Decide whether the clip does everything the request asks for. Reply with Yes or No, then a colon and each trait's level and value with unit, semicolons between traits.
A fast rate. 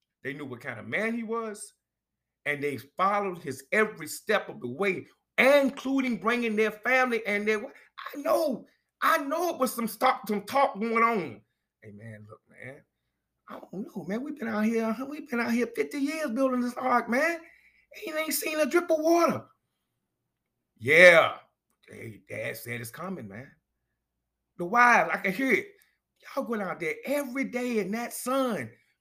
No: average, 180 wpm